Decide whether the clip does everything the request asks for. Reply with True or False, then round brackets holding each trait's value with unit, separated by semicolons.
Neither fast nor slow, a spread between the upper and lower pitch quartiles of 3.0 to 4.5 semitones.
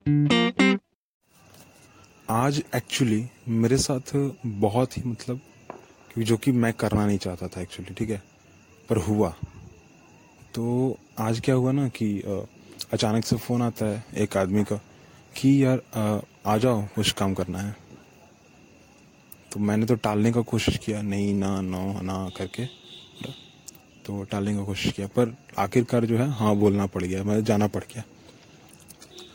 True (145 wpm; 3.5 semitones)